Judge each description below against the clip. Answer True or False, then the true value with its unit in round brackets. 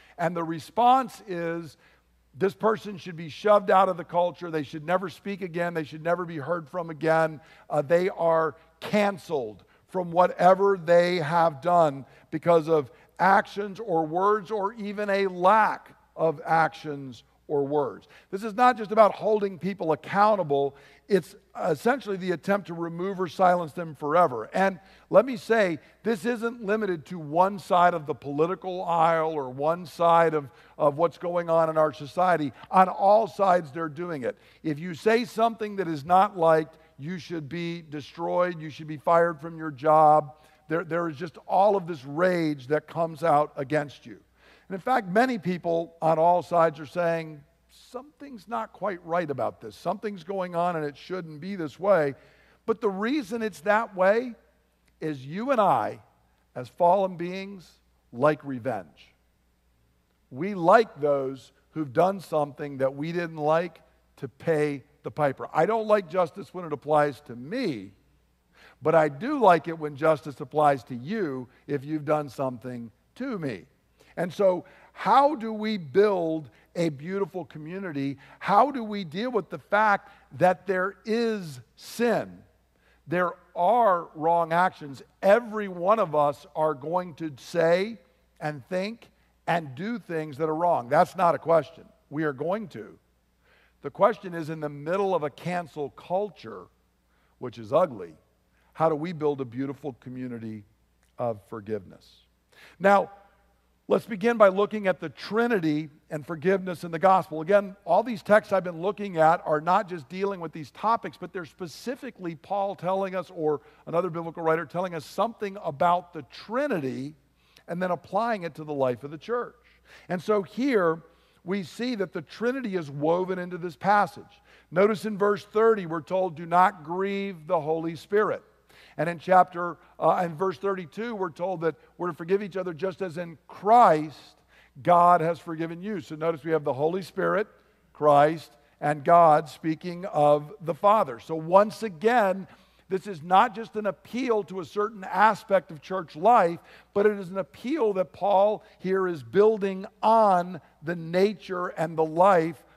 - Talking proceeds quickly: False (165 wpm)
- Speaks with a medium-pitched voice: True (175 Hz)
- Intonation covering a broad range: False (4.1 semitones)